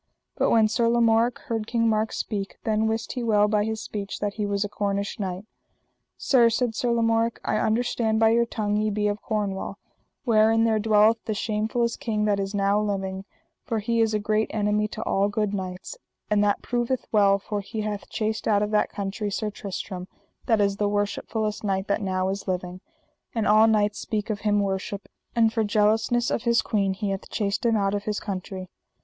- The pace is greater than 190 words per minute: Yes, fast, 205 wpm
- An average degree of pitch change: No, narrow, 1.7 semitones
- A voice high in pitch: Yes, high, 210 Hz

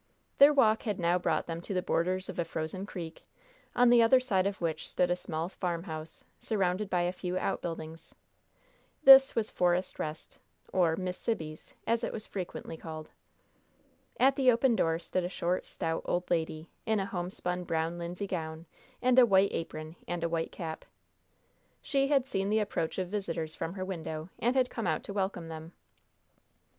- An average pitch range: Yes, average, 4.1 semitones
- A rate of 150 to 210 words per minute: Yes, average, 180 wpm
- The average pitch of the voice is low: No, medium, 180 Hz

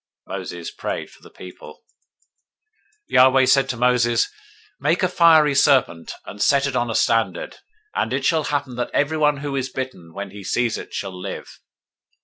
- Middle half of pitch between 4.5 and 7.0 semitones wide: No, average, 3.7 semitones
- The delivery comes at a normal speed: Yes, average, 175 wpm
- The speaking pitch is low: Yes, low, 130 Hz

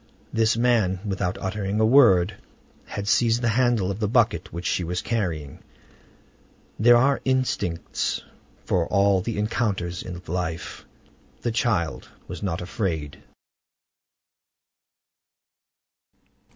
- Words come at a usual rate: No, slow, 110 wpm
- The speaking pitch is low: Yes, low, 100 Hz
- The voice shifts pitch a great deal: No, average, 4.5 semitones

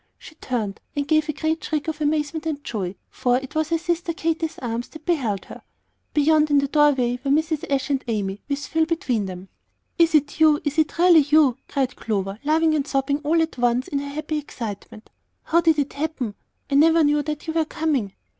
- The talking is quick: Yes, fast, 210 wpm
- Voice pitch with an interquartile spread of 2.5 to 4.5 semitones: Yes, average, 3.5 semitones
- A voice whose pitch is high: Yes, very high, 295 Hz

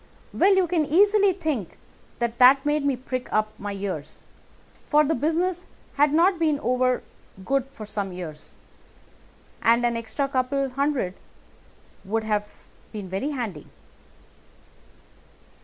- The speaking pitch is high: Yes, very high, 255 Hz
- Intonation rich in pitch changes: Yes, wide, 5.9 semitones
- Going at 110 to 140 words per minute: Yes, slow, 135 wpm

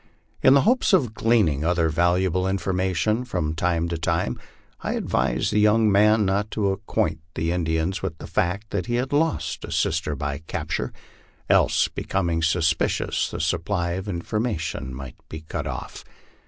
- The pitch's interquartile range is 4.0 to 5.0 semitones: Yes, average, 4.5 semitones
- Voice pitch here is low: Yes, very low, 90 Hz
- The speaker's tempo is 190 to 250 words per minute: No, average, 165 wpm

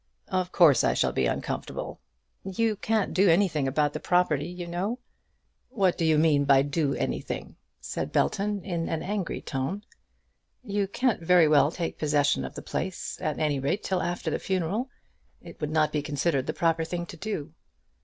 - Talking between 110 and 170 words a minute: No, average, 180 wpm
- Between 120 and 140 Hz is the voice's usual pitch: No, medium, 170 Hz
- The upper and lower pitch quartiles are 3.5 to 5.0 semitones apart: Yes, average, 4.1 semitones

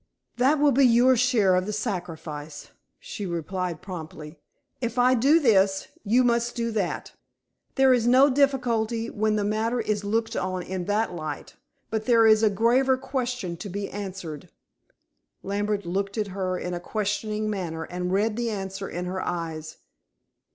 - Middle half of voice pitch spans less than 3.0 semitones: No, average, 4.4 semitones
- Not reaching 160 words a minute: No, average, 165 wpm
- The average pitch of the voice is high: Yes, high, 210 Hz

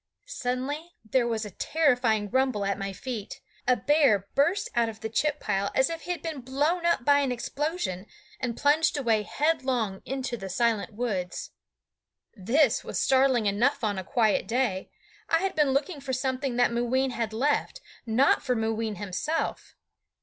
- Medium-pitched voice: No, very high, 250 Hz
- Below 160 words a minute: No, average, 170 wpm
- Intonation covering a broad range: No, average, 4.6 semitones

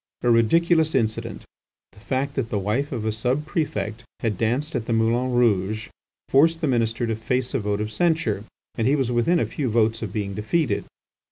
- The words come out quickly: No, average, 190 wpm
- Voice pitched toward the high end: No, low, 120 Hz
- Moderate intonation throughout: Yes, average, 4.2 semitones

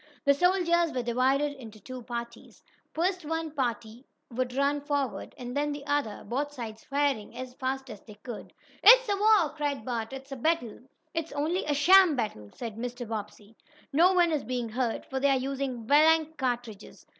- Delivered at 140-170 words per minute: No, average, 180 wpm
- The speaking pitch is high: Yes, very high, 270 Hz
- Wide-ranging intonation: No, average, 4.1 semitones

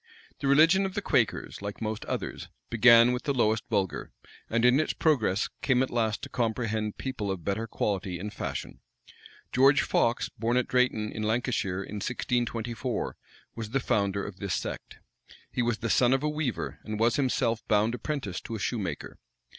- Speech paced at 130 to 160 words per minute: No, average, 180 wpm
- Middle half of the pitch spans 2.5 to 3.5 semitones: Yes, average, 3.1 semitones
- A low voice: Yes, low, 115 Hz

